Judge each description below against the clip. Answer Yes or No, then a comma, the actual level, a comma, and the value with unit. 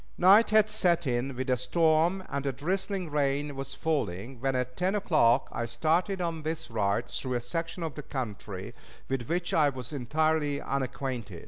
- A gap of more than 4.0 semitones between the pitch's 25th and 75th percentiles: Yes, average, 4.9 semitones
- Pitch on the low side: No, medium, 145 Hz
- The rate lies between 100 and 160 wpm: No, average, 175 wpm